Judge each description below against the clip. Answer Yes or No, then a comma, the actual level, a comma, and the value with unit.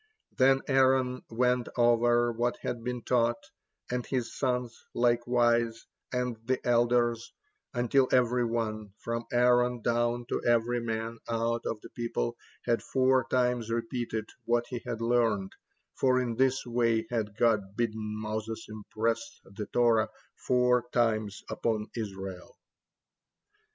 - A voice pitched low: Yes, low, 120 Hz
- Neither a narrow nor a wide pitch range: No, narrow, 1.5 semitones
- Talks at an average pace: No, slow, 130 wpm